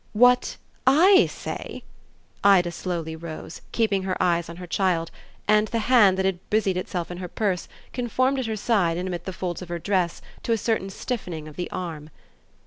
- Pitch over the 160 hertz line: Yes, medium, 185 Hz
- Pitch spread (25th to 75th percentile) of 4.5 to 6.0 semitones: No, average, 4.1 semitones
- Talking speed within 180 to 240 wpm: Yes, average, 190 wpm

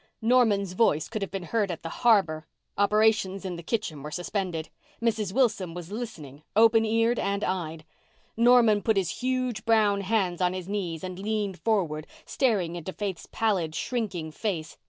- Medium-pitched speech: No, high, 200 Hz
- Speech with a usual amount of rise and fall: Yes, average, 4.2 semitones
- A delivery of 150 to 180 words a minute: Yes, average, 165 wpm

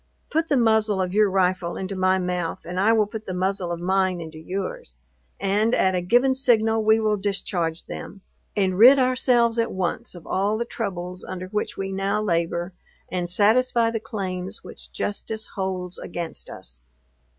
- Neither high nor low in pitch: No, high, 195 Hz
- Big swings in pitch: No, average, 3.4 semitones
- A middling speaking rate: Yes, average, 175 wpm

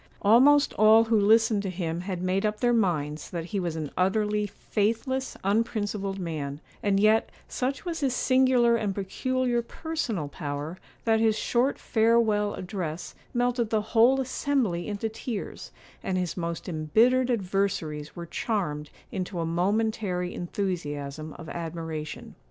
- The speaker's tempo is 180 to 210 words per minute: No, average, 140 wpm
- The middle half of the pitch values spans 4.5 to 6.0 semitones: Yes, average, 5.1 semitones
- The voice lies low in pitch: No, high, 205 Hz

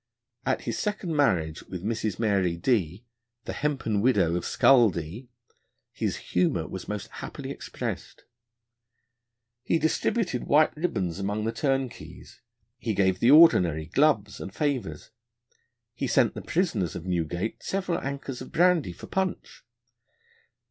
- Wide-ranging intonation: Yes, wide, 8.1 semitones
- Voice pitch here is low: Yes, low, 110 Hz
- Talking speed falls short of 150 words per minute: Yes, average, 140 wpm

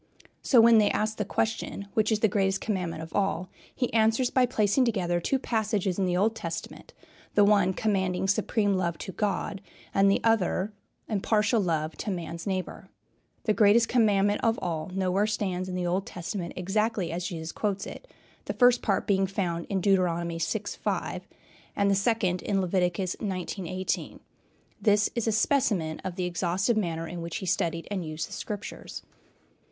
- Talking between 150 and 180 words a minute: Yes, average, 175 wpm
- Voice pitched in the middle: No, high, 195 Hz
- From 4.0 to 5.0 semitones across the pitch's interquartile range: No, average, 3.2 semitones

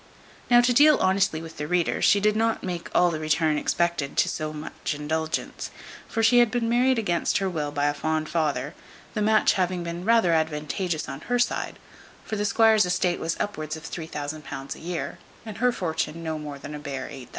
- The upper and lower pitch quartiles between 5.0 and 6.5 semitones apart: Yes, average, 5.3 semitones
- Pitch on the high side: No, medium, 170 Hz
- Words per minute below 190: No, fast, 205 wpm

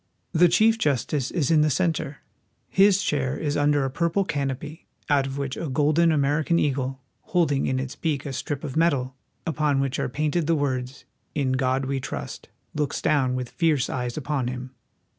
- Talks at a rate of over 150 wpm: Yes, average, 185 wpm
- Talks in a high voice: No, medium, 145 Hz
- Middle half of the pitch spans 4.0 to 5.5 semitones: No, average, 3.0 semitones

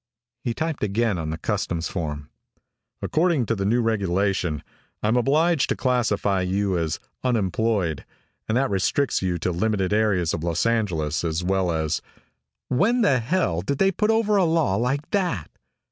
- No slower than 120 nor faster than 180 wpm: Yes, average, 165 wpm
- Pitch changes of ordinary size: No, wide, 7.1 semitones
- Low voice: Yes, low, 105 Hz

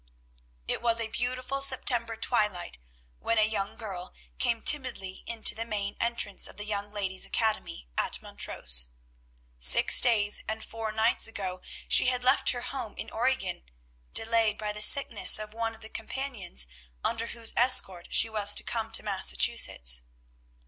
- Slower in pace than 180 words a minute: Yes, average, 155 wpm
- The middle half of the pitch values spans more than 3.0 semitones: No, narrow, 2.6 semitones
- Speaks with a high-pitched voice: Yes, high, 220 Hz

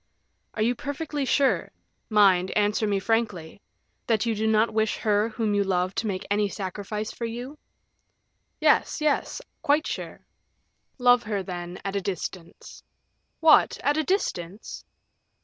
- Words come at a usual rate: Yes, average, 145 wpm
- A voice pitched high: Yes, high, 215 Hz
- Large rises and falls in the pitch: No, average, 3.7 semitones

